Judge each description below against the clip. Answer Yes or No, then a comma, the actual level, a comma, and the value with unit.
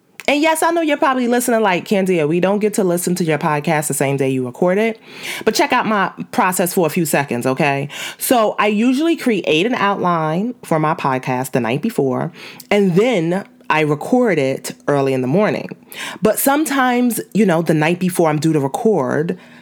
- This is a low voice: No, medium, 185 Hz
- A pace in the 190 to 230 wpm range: Yes, average, 200 wpm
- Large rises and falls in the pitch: Yes, wide, 6.6 semitones